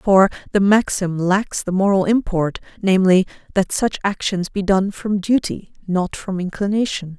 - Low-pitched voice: No, high, 195 Hz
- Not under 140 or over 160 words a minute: Yes, average, 150 wpm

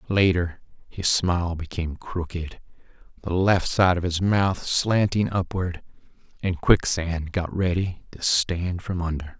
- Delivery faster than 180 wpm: No, slow, 135 wpm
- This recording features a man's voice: Yes, male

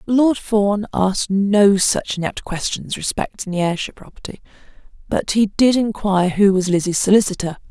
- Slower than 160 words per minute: Yes, average, 150 wpm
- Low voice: No, high, 200 Hz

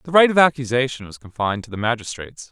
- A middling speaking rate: No, fast, 215 wpm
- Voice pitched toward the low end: Yes, low, 125 Hz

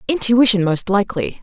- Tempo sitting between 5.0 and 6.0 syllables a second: Yes, 5.5 syllables/s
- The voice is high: Yes, high, 210 Hz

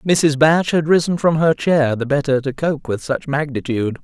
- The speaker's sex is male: Yes, male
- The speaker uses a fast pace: Yes, fast, 210 wpm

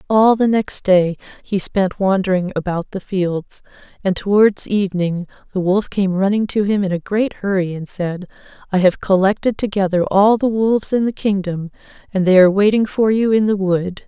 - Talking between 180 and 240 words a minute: Yes, average, 190 wpm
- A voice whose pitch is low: No, high, 195 Hz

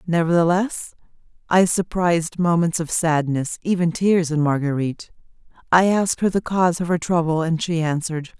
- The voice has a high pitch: No, medium, 170 Hz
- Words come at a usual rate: Yes, average, 150 wpm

